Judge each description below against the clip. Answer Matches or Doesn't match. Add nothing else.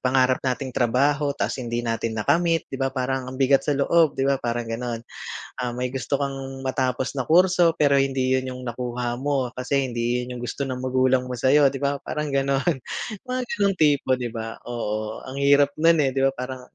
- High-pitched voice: Doesn't match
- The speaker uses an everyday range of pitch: Doesn't match